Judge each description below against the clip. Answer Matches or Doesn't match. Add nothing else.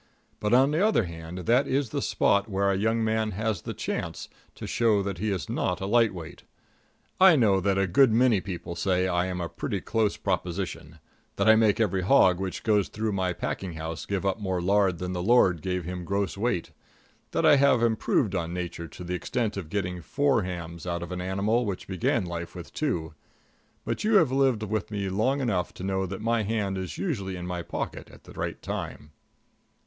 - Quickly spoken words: Matches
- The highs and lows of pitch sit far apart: Doesn't match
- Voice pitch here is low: Matches